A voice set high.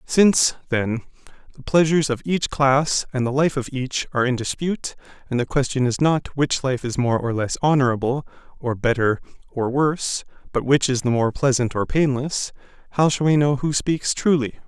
No: low, 135 Hz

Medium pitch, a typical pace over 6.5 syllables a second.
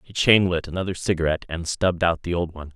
No: very low, 85 Hz; 6.9 syllables/s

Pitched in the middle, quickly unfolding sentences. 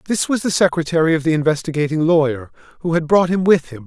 Yes: medium, 160 Hz; fast, 220 wpm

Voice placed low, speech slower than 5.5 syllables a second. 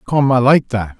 Yes: low, 125 Hz; 4.9 syllables/s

